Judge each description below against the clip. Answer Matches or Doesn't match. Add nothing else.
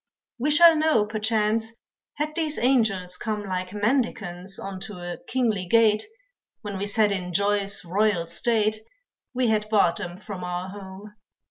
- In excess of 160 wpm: Doesn't match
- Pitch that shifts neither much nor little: Matches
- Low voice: Doesn't match